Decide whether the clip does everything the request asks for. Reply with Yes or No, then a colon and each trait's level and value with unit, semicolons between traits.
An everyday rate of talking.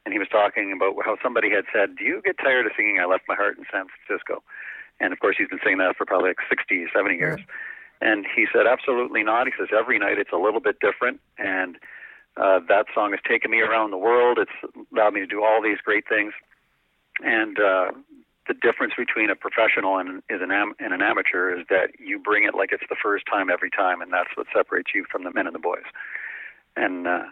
No: fast, 230 wpm